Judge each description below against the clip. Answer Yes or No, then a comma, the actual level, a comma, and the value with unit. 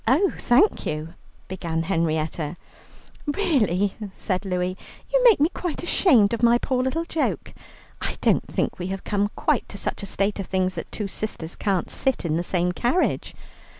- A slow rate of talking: No, average, 175 wpm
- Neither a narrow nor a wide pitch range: No, wide, 6.7 semitones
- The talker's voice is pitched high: Yes, high, 200 Hz